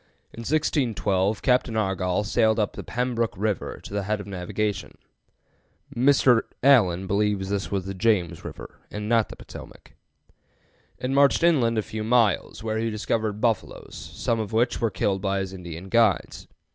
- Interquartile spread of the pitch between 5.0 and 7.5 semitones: No, average, 3.1 semitones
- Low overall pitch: Yes, low, 110 Hz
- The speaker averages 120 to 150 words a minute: No, average, 160 wpm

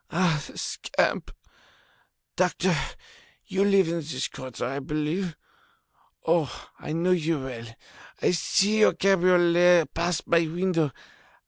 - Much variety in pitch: No, average, 3.1 semitones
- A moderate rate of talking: No, slow, 120 wpm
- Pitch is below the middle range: No, medium, 170 Hz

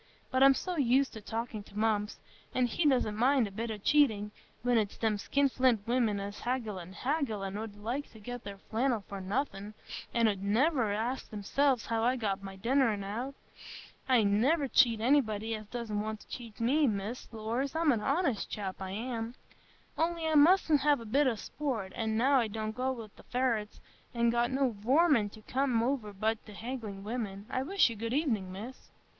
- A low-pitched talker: No, high, 230 Hz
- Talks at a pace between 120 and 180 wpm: No, average, 195 wpm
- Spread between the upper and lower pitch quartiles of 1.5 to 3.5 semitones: No, average, 4.0 semitones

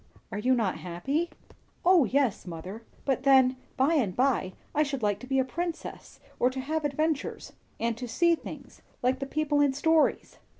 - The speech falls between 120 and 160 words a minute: No, average, 175 wpm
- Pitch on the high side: Yes, very high, 270 Hz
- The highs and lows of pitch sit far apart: No, average, 4.5 semitones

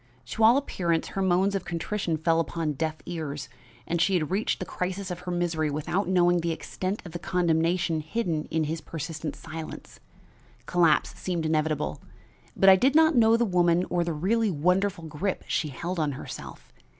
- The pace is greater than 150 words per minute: Yes, average, 180 wpm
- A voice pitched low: No, medium, 175 Hz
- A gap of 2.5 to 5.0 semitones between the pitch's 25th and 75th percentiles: Yes, average, 2.9 semitones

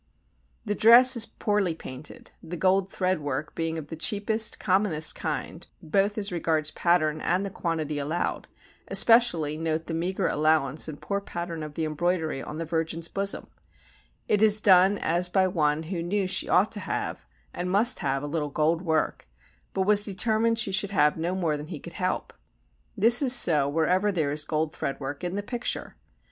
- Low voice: No, medium, 175 Hz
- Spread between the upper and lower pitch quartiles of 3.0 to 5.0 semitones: Yes, average, 4.3 semitones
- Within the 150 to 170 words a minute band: No, average, 185 wpm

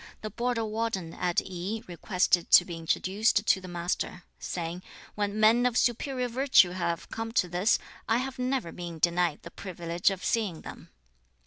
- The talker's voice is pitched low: No, high, 190 Hz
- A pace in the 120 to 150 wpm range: No, average, 165 wpm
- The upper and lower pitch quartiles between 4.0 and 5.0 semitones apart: Yes, average, 4.6 semitones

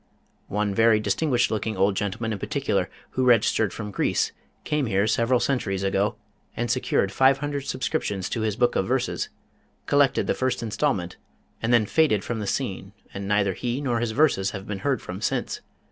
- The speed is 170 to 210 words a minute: Yes, average, 180 wpm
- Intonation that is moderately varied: Yes, average, 4.4 semitones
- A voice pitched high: No, low, 110 Hz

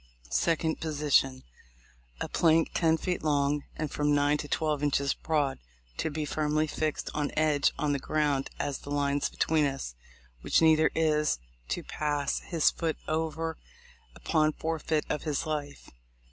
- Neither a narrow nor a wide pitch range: No, narrow, 1.6 semitones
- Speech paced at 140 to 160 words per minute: Yes, average, 150 wpm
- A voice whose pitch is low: No, medium, 150 Hz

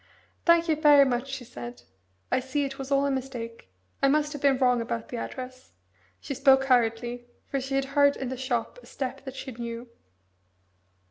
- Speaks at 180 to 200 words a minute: Yes, average, 195 wpm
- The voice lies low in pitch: No, very high, 265 Hz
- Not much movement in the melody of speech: Yes, narrow, 2.3 semitones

